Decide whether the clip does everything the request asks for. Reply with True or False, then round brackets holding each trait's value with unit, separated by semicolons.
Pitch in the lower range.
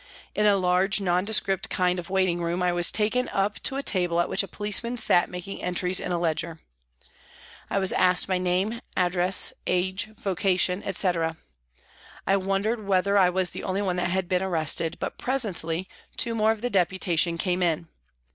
False (185 Hz)